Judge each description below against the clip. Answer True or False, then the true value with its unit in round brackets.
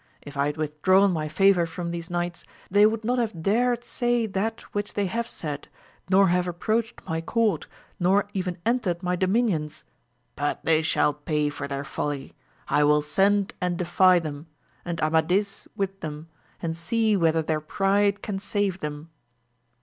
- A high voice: False (180 Hz)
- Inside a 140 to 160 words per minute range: False (170 wpm)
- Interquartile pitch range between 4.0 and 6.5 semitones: True (4.6 semitones)